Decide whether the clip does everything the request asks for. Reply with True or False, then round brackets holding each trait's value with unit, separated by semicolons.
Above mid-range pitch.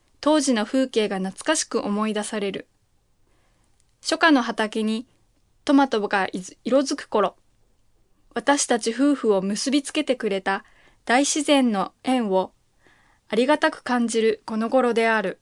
True (235 Hz)